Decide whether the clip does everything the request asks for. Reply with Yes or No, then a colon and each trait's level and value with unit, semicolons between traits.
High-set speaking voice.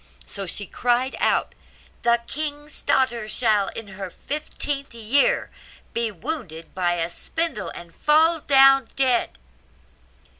Yes: high, 240 Hz